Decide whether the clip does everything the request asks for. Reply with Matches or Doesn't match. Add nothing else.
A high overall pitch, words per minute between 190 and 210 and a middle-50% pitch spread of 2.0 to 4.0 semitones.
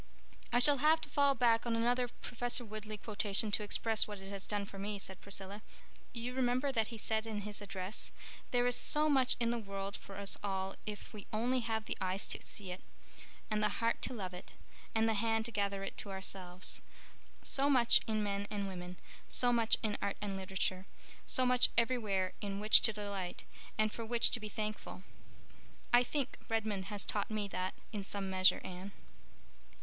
Matches